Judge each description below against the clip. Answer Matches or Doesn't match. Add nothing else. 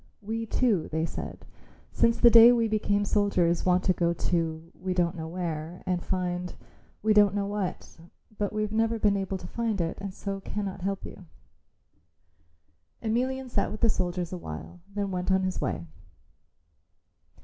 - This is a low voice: Doesn't match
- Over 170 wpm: Doesn't match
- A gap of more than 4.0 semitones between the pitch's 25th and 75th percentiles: Doesn't match